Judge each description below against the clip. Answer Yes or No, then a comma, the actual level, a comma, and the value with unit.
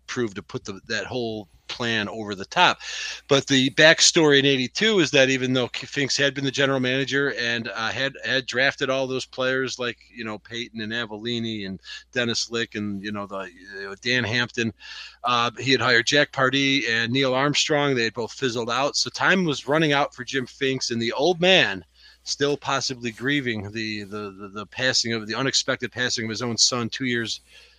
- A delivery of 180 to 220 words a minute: Yes, average, 200 wpm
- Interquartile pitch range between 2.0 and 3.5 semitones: Yes, average, 3.0 semitones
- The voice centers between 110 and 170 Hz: Yes, low, 125 Hz